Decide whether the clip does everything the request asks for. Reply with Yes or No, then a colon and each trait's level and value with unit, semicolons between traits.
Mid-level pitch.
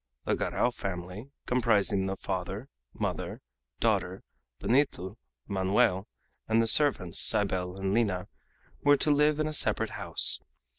No: low, 100 Hz